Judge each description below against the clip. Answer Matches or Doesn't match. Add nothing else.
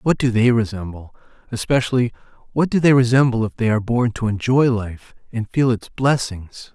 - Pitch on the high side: Doesn't match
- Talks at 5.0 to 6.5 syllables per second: Matches